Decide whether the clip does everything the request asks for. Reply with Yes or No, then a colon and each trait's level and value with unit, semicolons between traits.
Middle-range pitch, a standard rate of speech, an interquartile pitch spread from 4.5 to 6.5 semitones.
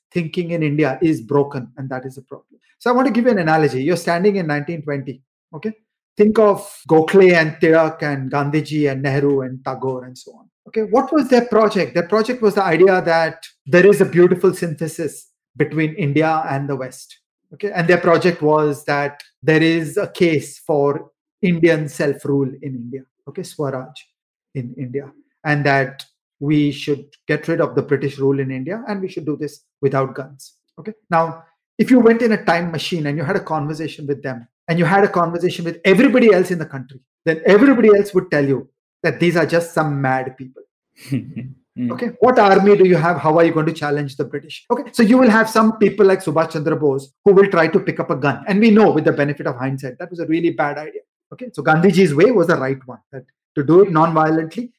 No: medium, 160 Hz; fast, 215 wpm; average, 5.2 semitones